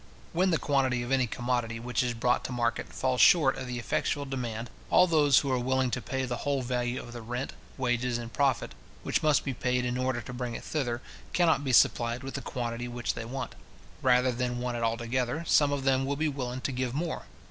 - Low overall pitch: Yes, low, 125 Hz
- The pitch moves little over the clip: Yes, narrow, 1.8 semitones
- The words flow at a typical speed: No, fast, 225 wpm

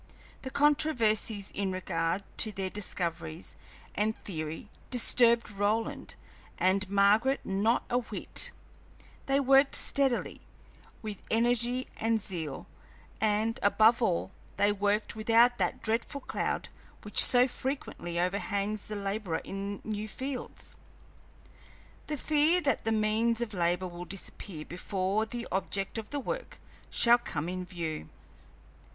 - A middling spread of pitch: Yes, average, 3.8 semitones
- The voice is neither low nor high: No, high, 215 Hz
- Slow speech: Yes, slow, 125 wpm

